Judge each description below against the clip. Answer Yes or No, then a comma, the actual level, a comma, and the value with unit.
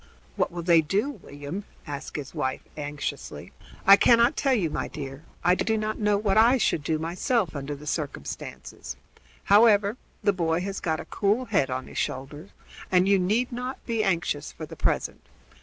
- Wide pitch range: Yes, wide, 6.4 semitones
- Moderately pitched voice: Yes, medium, 180 Hz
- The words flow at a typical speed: Yes, average, 180 wpm